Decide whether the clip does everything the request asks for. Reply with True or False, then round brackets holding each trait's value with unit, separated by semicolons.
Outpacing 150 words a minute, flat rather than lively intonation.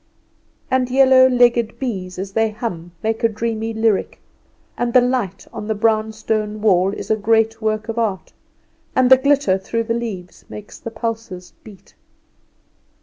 True (160 wpm; 2.1 semitones)